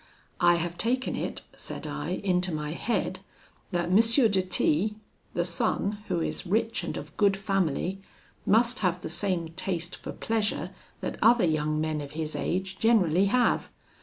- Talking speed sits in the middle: Yes, average, 165 wpm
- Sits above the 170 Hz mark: Yes, medium, 185 Hz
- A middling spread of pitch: Yes, average, 4.0 semitones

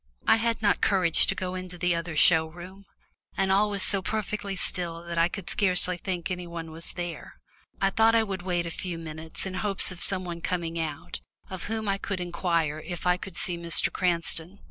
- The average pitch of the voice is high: No, medium, 180 Hz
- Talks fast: Yes, fast, 210 wpm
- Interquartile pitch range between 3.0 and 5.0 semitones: No, narrow, 2.4 semitones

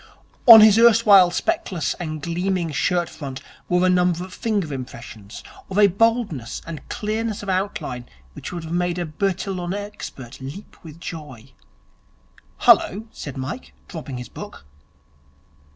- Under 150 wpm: Yes, slow, 135 wpm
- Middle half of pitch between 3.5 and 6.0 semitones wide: Yes, average, 5.2 semitones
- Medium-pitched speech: Yes, medium, 180 Hz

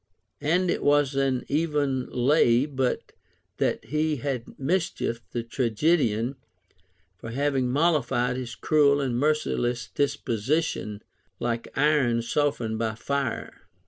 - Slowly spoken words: Yes, slow, 110 wpm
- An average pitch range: Yes, average, 3.7 semitones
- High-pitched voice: No, low, 135 Hz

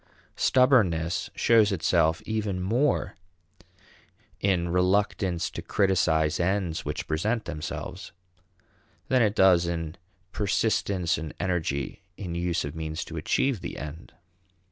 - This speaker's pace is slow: Yes, slow, 115 wpm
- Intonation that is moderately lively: Yes, average, 3.8 semitones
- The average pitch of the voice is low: Yes, very low, 90 Hz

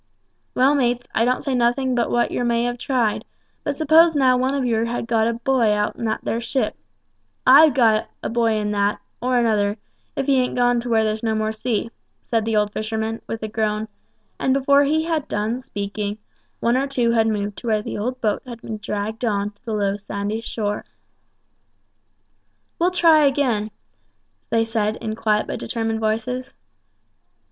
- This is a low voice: No, high, 230 Hz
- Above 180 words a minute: Yes, average, 190 wpm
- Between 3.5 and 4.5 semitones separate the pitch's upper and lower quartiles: No, average, 2.9 semitones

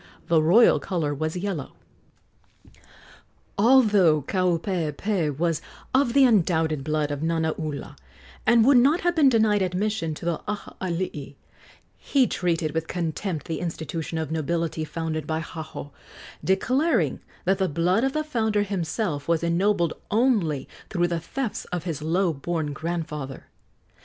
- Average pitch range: Yes, average, 4.7 semitones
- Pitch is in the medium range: Yes, medium, 170 Hz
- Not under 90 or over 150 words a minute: Yes, slow, 135 wpm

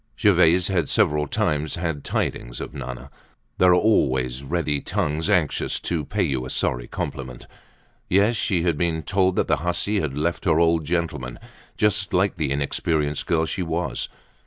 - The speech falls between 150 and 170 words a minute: Yes, average, 165 wpm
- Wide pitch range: No, average, 3.9 semitones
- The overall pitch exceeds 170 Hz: No, very low, 80 Hz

